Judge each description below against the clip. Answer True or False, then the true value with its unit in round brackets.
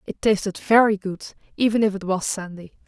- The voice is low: False (200 Hz)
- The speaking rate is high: False (190 wpm)